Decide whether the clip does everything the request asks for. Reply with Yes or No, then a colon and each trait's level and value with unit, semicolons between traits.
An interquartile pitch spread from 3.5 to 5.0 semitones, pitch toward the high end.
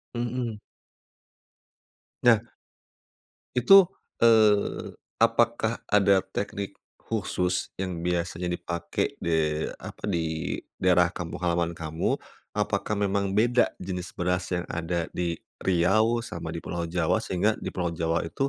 No: average, 3.8 semitones; very low, 90 Hz